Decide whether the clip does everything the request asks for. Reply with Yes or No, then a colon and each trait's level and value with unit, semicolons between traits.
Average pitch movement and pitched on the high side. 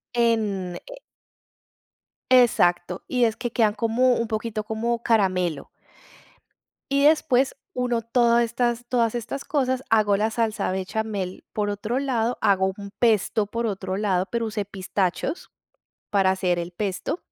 Yes: average, 3.3 semitones; high, 220 Hz